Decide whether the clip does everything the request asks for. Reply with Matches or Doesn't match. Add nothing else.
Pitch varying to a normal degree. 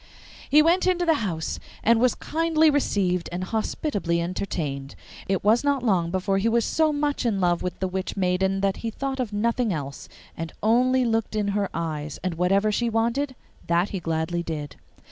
Doesn't match